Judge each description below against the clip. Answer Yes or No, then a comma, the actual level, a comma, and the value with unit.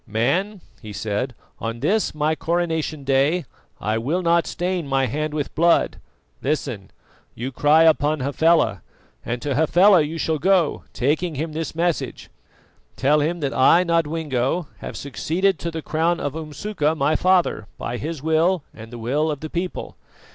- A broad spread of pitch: No, average, 3.8 semitones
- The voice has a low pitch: No, medium, 155 Hz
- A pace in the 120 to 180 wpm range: Yes, average, 160 wpm